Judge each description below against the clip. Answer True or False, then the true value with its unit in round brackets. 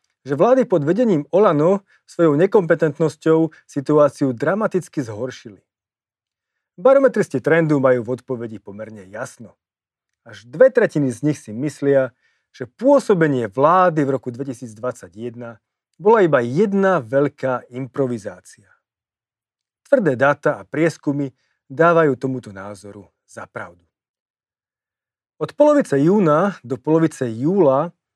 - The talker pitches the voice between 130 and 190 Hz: True (140 Hz)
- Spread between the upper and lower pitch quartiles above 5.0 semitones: True (5.4 semitones)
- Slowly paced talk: True (105 wpm)